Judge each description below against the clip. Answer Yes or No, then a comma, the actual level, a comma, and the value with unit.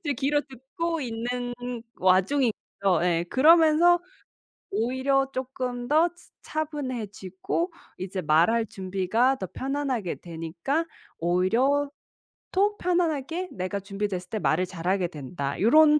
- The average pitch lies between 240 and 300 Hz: Yes, high, 245 Hz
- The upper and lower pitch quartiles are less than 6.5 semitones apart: No, wide, 7.8 semitones